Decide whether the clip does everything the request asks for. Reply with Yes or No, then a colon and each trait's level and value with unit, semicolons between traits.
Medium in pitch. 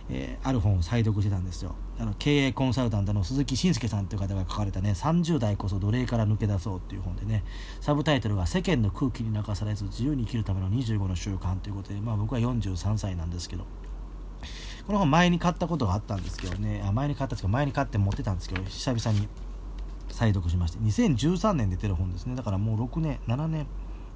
No: low, 105 Hz